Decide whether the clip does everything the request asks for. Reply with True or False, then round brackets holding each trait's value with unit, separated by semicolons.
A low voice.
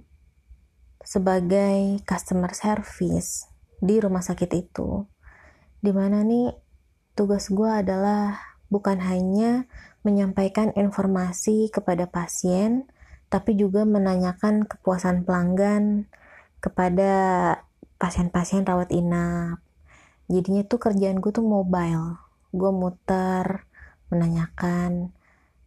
False (190 Hz)